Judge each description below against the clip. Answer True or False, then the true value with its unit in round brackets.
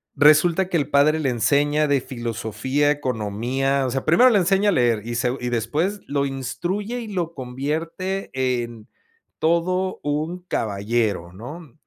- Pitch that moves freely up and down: True (5.7 semitones)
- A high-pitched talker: False (140 Hz)